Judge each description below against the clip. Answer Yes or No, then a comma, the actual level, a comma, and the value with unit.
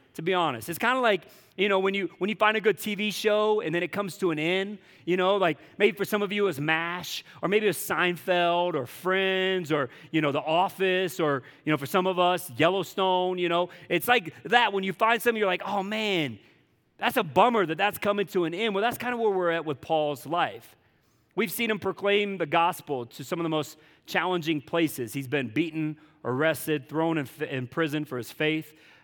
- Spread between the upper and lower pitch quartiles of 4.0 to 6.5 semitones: Yes, average, 4.4 semitones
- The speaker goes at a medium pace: No, fast, 230 wpm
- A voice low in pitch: No, medium, 180 Hz